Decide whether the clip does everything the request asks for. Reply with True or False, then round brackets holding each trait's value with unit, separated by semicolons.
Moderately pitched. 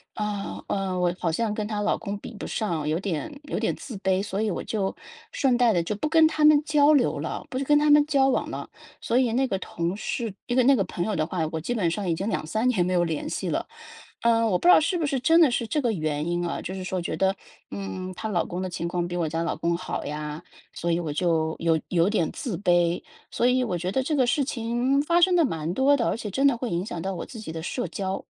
False (200 Hz)